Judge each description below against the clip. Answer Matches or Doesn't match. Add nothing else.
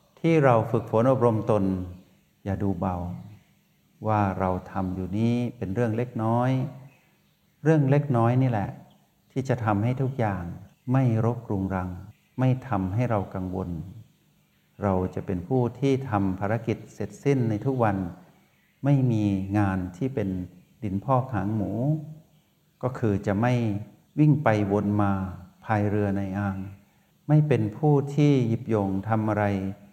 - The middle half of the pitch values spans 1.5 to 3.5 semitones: Doesn't match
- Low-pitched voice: Matches